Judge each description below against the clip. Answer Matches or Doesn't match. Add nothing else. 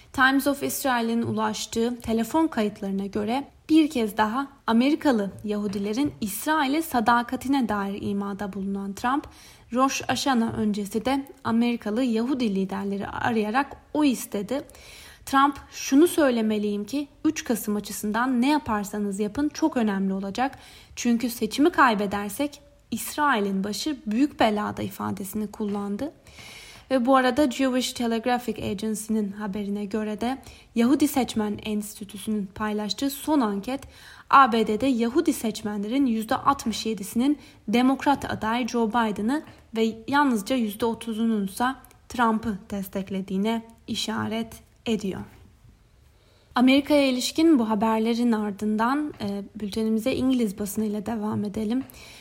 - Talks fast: Doesn't match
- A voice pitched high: Matches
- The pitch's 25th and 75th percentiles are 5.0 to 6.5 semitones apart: Doesn't match